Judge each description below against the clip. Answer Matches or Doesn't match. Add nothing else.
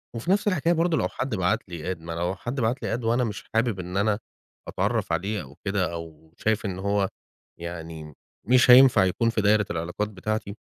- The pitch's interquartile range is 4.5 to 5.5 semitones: Matches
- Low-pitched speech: Matches